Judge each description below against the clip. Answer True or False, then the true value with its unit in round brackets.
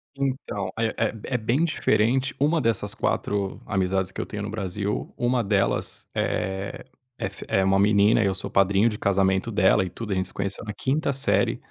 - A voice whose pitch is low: True (105 Hz)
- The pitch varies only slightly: False (3.2 semitones)